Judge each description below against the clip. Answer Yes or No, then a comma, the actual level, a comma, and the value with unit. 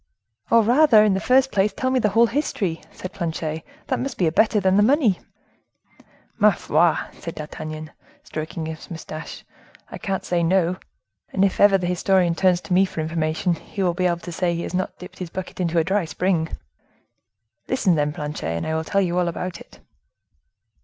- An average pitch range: Yes, average, 3.4 semitones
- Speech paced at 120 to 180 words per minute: No, average, 195 wpm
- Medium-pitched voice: Yes, medium, 180 Hz